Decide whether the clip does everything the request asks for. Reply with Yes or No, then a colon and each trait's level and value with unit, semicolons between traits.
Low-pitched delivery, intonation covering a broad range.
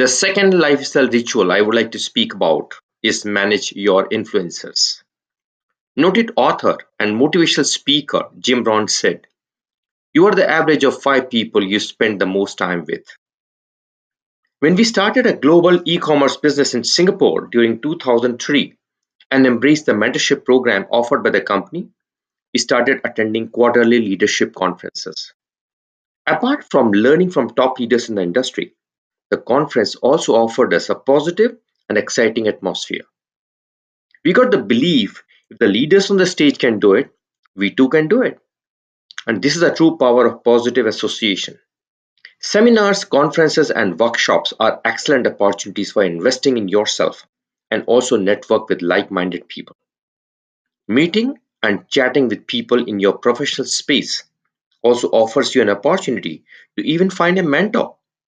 Yes: low, 125 Hz; wide, 6.2 semitones